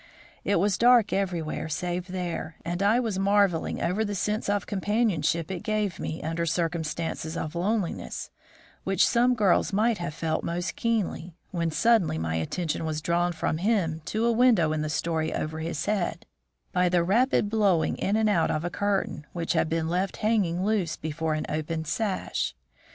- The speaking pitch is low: No, medium, 175 Hz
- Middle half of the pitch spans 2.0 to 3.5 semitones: No, average, 4.3 semitones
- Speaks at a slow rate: No, average, 175 wpm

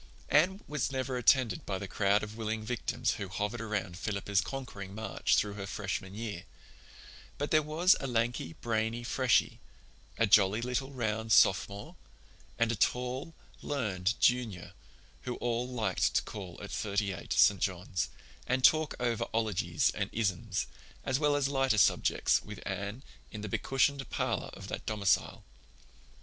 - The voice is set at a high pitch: No, low, 110 Hz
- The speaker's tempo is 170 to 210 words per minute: No, average, 155 wpm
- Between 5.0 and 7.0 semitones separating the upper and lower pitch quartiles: No, average, 4.2 semitones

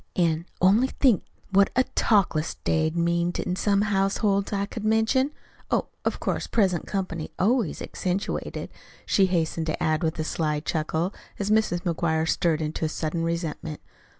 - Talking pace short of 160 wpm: Yes, average, 150 wpm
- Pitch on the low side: No, medium, 175 Hz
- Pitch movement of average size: Yes, average, 3.9 semitones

